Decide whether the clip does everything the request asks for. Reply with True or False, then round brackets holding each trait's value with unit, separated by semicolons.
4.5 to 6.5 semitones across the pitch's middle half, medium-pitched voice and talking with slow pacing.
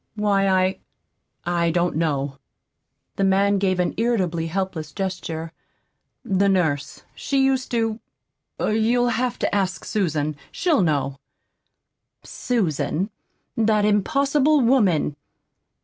False (5.4 semitones; 195 Hz; 105 wpm)